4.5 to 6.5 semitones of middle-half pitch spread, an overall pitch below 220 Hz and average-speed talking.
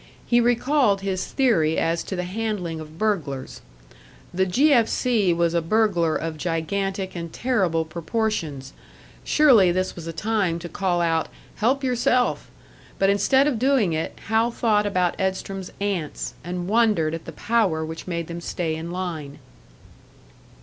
Yes: average, 5.0 semitones; medium, 185 Hz; average, 155 wpm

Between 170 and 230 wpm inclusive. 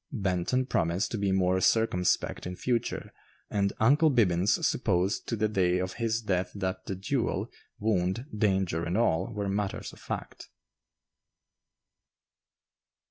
No: slow, 135 wpm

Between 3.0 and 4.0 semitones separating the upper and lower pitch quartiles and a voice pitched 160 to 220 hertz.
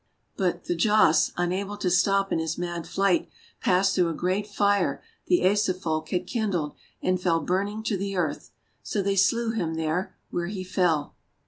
No: narrow, 2.5 semitones; medium, 185 Hz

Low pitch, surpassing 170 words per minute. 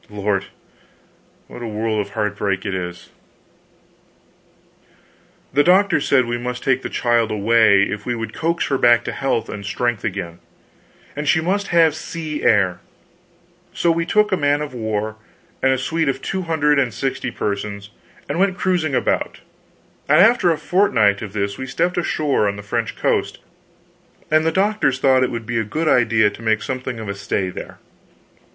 Yes: low, 125 Hz; average, 180 wpm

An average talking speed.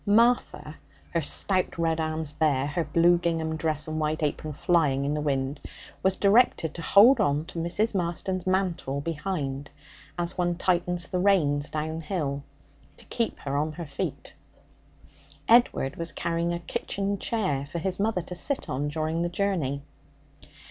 Yes: average, 155 wpm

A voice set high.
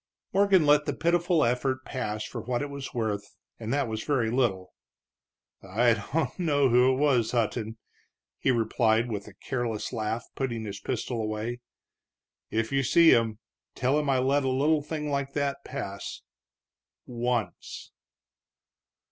No: low, 125 Hz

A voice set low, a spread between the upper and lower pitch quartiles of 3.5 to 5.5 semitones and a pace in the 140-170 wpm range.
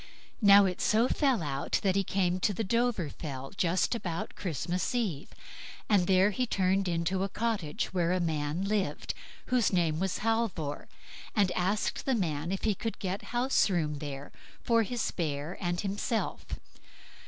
No: high, 190 Hz; average, 4.3 semitones; average, 160 wpm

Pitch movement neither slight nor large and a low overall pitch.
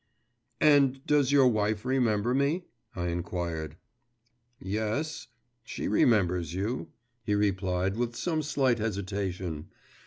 No: wide, 6.0 semitones; low, 105 Hz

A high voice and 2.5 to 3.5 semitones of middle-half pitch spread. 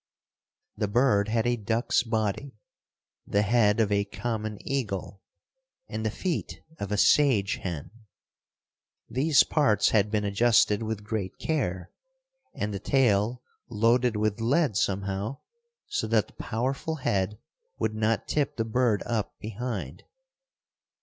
No: low, 110 Hz; average, 3.1 semitones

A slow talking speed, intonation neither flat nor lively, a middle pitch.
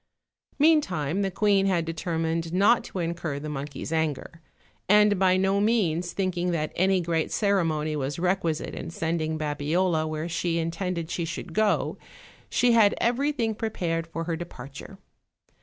No: average, 150 wpm; average, 3.5 semitones; medium, 170 Hz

